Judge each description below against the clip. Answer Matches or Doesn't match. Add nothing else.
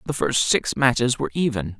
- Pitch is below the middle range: Matches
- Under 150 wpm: Doesn't match